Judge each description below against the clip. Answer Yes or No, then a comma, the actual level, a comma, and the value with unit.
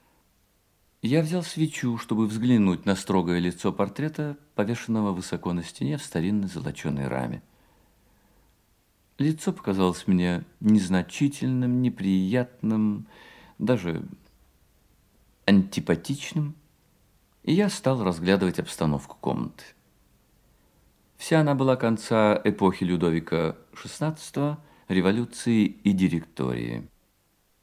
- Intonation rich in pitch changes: Yes, wide, 5.7 semitones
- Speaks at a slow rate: Yes, slow, 85 wpm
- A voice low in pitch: Yes, low, 100 Hz